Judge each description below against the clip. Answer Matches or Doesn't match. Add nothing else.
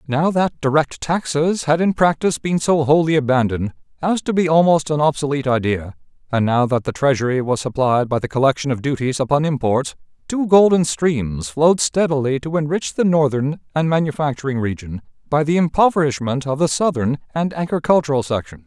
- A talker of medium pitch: Matches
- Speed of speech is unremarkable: Matches